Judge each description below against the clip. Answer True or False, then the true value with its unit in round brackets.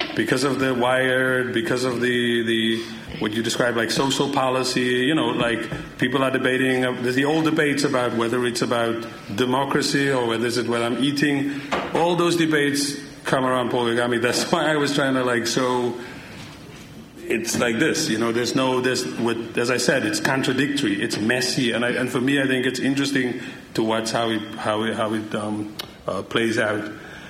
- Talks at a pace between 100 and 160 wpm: False (195 wpm)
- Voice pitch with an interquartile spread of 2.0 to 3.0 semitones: True (2.7 semitones)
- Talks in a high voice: False (125 Hz)